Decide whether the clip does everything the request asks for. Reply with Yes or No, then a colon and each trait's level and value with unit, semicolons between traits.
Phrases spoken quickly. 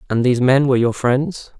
Yes: fast, 225 wpm